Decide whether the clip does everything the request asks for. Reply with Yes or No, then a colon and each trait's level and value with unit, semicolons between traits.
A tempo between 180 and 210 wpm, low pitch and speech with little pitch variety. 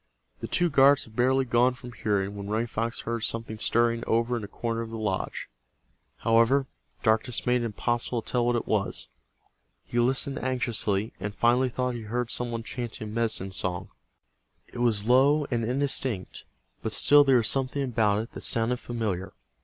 Yes: average, 185 wpm; low, 115 Hz; narrow, 2.3 semitones